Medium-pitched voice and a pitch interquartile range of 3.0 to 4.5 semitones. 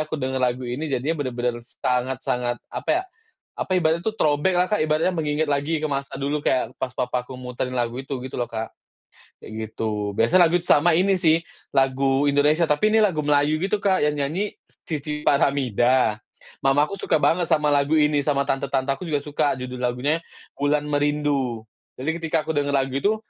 Yes: medium, 145 Hz; average, 3.3 semitones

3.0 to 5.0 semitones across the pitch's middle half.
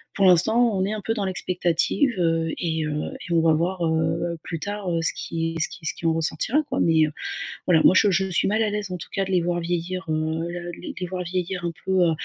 No: narrow, 2.6 semitones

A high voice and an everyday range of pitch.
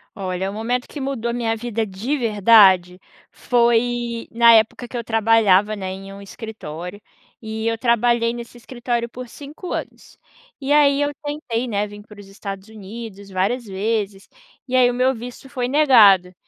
Yes: high, 225 Hz; average, 3.3 semitones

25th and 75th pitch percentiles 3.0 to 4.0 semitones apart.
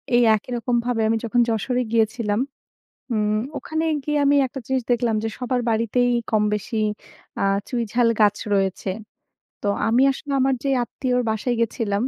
No: narrow, 2.5 semitones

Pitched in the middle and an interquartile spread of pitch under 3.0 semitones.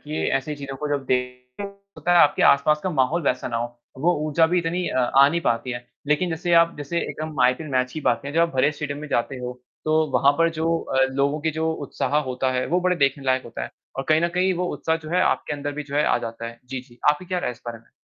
No: medium, 145 Hz; average, 4.1 semitones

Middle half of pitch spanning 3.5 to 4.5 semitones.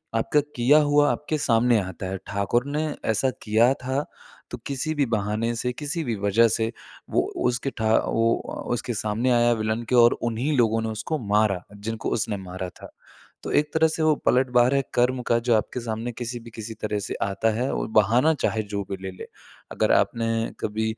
No: average, 2.9 semitones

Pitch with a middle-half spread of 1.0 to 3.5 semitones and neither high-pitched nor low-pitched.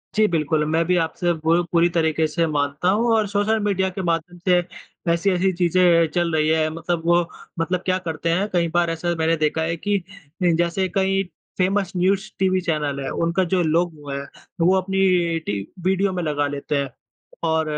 Yes: average, 2.7 semitones; medium, 170 Hz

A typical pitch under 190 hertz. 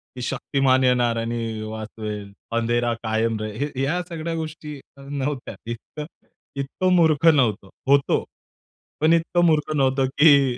Yes: low, 135 Hz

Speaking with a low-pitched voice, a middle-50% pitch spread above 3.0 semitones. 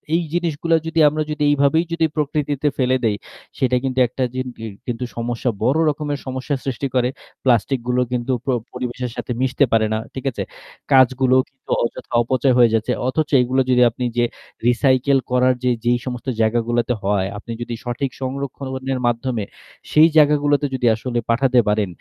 No: low, 130 Hz; narrow, 2.5 semitones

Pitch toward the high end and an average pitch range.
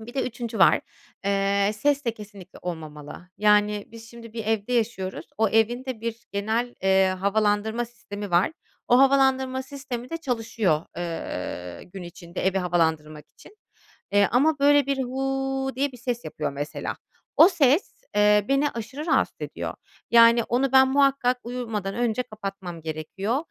Yes: high, 225 Hz; average, 4.9 semitones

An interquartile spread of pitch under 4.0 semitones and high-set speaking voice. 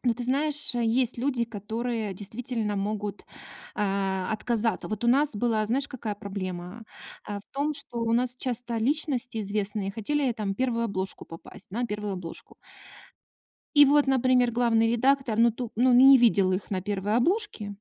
Yes: average, 3.5 semitones; high, 230 Hz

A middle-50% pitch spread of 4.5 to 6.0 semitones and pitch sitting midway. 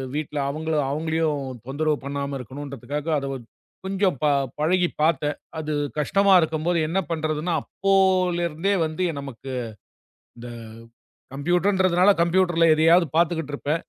No: average, 3.3 semitones; medium, 160 Hz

